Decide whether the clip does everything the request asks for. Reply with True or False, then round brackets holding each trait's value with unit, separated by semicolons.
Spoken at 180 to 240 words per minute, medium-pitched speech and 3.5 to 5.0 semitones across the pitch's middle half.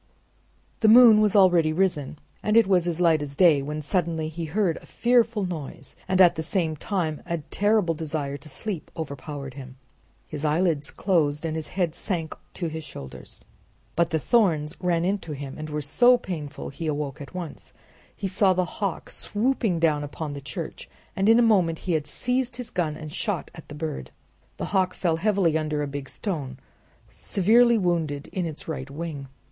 True (190 wpm; 165 Hz; 4.2 semitones)